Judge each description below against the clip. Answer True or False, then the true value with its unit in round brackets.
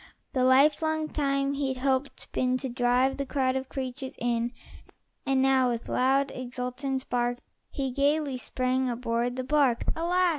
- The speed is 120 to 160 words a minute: True (150 wpm)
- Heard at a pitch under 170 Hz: False (260 Hz)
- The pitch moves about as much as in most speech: False (1.7 semitones)